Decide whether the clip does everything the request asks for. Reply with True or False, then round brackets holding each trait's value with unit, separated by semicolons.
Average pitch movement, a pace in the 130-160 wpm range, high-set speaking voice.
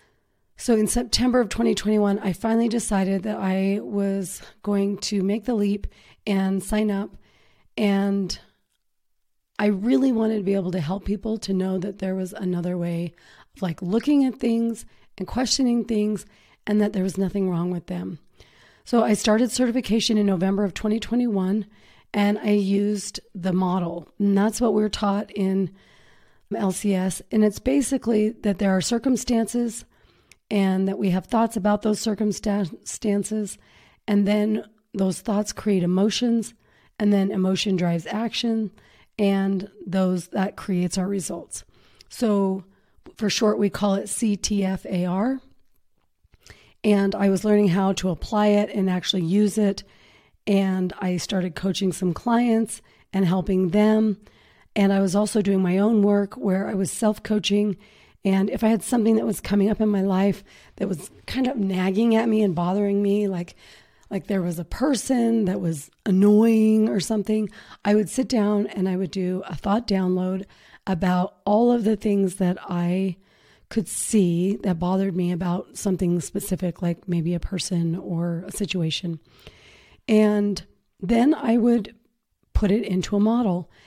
False (2.3 semitones; 155 wpm; 200 Hz)